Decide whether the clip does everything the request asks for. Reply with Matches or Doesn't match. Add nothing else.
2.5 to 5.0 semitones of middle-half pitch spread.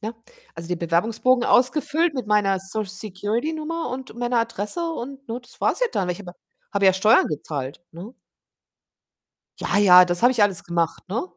Doesn't match